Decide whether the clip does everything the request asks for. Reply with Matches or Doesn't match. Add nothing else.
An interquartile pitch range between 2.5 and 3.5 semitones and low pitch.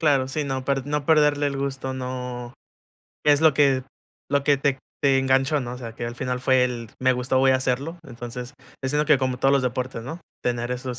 Doesn't match